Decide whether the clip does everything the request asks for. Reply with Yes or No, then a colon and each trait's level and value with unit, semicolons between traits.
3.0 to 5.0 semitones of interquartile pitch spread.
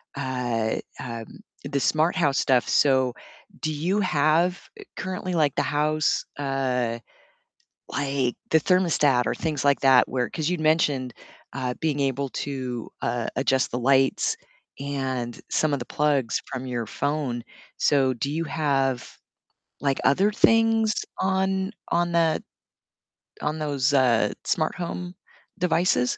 Yes: average, 3.8 semitones